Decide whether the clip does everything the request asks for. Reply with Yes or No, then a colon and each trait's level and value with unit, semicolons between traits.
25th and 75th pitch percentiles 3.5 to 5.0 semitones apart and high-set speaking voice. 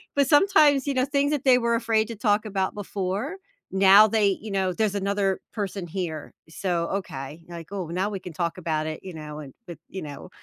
Yes: average, 4.5 semitones; high, 195 Hz